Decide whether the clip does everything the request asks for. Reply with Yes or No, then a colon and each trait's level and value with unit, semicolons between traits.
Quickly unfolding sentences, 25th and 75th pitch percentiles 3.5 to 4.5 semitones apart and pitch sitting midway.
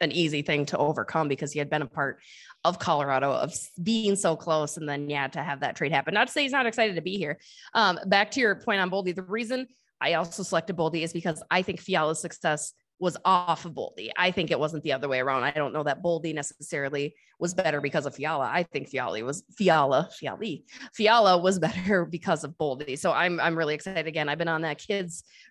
Yes: fast, 235 wpm; average, 3.9 semitones; medium, 165 Hz